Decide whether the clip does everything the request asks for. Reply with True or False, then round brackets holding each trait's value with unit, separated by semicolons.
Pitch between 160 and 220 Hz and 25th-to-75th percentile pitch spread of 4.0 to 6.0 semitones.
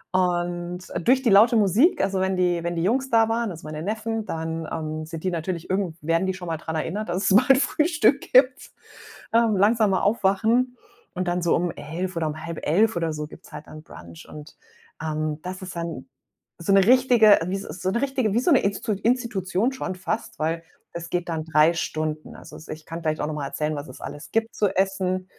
True (185 Hz; 5.2 semitones)